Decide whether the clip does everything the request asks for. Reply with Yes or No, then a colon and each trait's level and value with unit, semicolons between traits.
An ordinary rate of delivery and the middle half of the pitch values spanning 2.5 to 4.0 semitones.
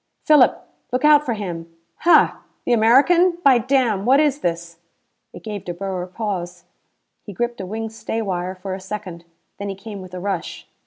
No: average, 180 wpm; average, 5.1 semitones